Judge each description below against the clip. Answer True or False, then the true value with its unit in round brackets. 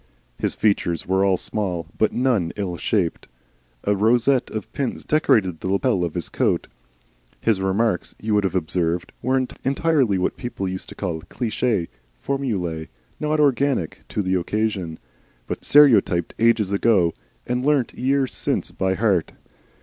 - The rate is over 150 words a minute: False (145 wpm)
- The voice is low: True (105 Hz)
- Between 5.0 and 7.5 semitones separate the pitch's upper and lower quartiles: True (5.3 semitones)